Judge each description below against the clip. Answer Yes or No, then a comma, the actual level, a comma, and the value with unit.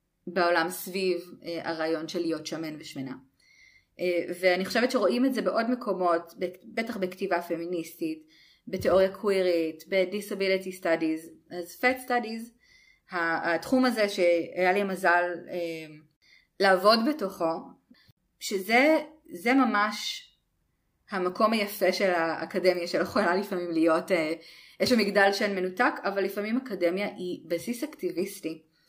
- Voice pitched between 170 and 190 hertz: Yes, medium, 185 Hz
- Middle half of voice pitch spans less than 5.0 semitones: Yes, average, 3.8 semitones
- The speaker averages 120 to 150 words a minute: No, average, 110 wpm